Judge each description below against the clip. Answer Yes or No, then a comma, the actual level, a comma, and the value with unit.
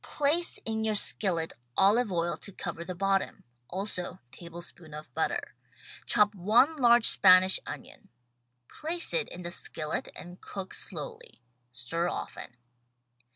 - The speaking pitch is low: No, high, 195 Hz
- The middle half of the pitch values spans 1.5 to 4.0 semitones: No, average, 5.0 semitones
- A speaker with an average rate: No, slow, 130 wpm